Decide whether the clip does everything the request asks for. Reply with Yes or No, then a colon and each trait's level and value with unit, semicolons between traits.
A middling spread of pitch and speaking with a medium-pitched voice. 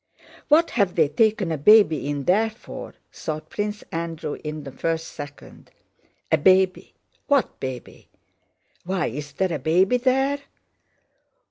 No: wide, 6.0 semitones; medium, 175 Hz